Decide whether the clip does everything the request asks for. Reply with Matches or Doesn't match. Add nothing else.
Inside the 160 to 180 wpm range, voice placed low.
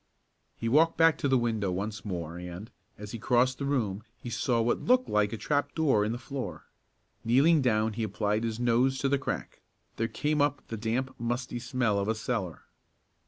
Doesn't match